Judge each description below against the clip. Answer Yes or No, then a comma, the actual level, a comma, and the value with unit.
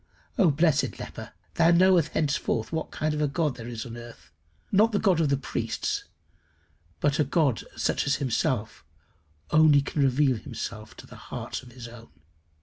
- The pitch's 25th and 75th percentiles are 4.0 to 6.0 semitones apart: Yes, average, 5.1 semitones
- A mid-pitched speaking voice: Yes, medium, 145 Hz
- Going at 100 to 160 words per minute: No, average, 175 wpm